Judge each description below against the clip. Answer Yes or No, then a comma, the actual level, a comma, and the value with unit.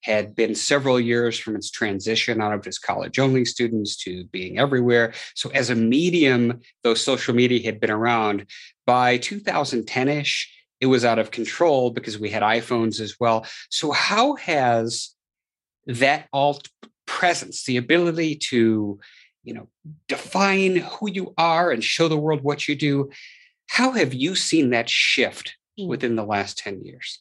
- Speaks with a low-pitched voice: Yes, low, 125 Hz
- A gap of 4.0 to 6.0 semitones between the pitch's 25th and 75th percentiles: Yes, average, 4.6 semitones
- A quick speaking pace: No, average, 160 wpm